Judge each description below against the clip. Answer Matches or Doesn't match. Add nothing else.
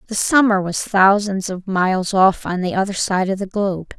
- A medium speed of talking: Doesn't match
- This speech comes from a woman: Matches